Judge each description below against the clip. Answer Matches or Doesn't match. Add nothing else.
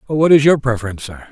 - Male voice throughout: Matches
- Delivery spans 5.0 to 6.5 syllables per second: Doesn't match